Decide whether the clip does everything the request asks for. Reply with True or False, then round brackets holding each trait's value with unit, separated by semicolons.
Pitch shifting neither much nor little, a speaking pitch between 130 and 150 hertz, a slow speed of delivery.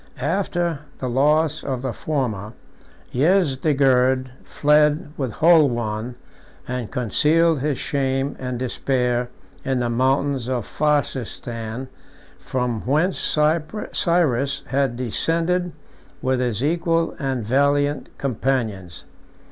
True (3.6 semitones; 135 Hz; 100 wpm)